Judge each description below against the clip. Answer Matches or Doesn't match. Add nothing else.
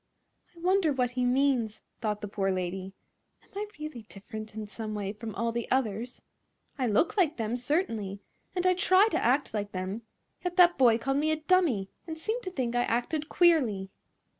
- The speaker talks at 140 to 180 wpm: Doesn't match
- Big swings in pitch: Matches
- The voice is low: Doesn't match